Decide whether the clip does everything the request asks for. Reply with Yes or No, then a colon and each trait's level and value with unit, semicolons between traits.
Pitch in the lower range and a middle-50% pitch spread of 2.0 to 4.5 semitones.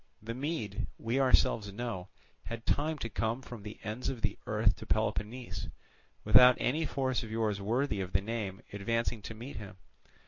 Yes: low, 115 Hz; average, 3.3 semitones